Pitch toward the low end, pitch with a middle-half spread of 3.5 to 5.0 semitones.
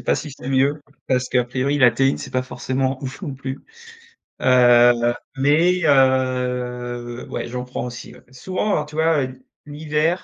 No: low, 130 Hz; average, 2.7 semitones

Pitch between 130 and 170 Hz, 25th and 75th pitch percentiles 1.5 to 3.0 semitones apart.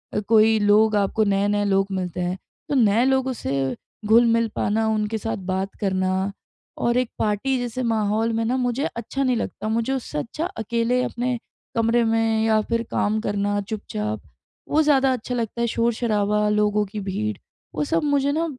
No: high, 220 Hz; narrow, 2.6 semitones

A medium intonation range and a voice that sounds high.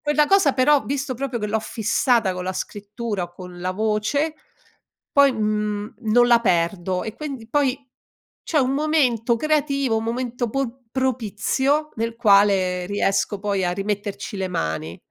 Yes: average, 5.0 semitones; high, 225 Hz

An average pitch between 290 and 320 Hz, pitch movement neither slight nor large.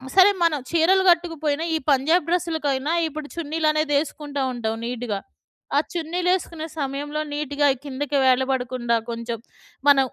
Yes: very high, 295 Hz; average, 3.6 semitones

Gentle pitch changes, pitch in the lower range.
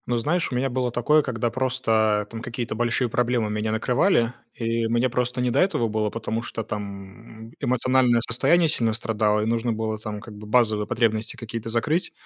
Yes: narrow, 2.2 semitones; low, 115 Hz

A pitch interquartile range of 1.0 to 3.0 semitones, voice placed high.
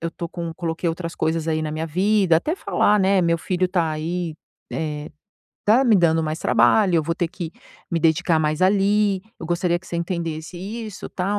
No: average, 2.7 semitones; medium, 170 Hz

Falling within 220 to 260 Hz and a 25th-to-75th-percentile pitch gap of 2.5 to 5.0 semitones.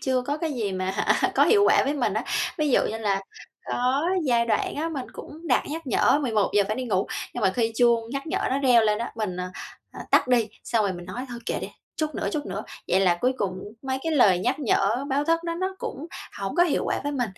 No: high, 245 Hz; wide, 5.5 semitones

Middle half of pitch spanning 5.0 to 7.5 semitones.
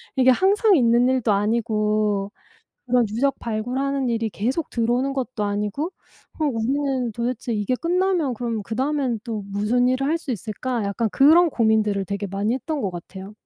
No: average, 4.3 semitones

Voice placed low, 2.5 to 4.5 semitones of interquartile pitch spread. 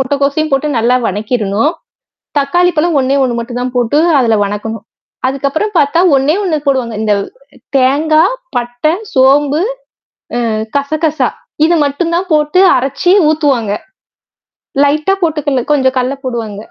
No: very high, 275 Hz; average, 3.9 semitones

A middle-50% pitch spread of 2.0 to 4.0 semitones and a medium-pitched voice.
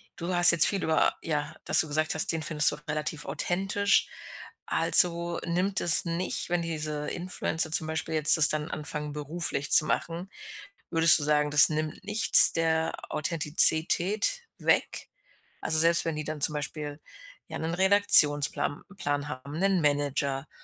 Yes: narrow, 2.4 semitones; medium, 160 Hz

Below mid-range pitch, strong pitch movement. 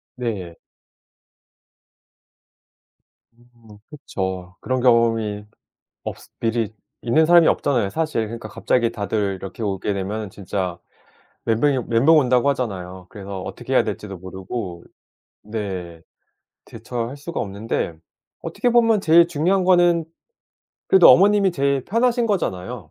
Yes: low, 115 Hz; wide, 7.3 semitones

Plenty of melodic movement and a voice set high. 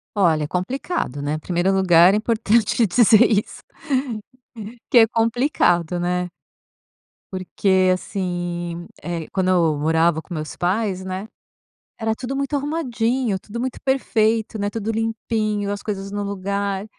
No: average, 4.2 semitones; high, 200 Hz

